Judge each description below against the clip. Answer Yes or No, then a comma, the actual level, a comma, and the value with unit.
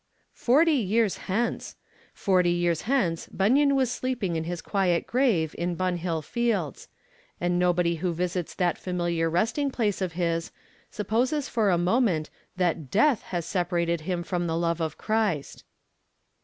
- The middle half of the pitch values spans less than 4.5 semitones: No, average, 4.8 semitones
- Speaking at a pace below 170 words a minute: Yes, average, 145 wpm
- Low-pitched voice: No, medium, 180 Hz